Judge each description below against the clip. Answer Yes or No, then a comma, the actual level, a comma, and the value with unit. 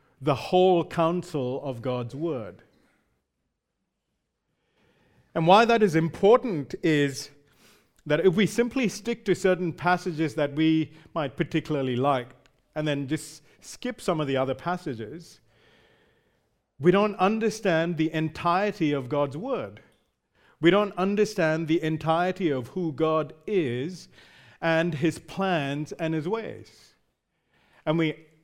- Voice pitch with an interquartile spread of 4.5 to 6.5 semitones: No, average, 3.7 semitones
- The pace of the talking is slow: Yes, slow, 125 wpm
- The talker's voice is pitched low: No, medium, 160 Hz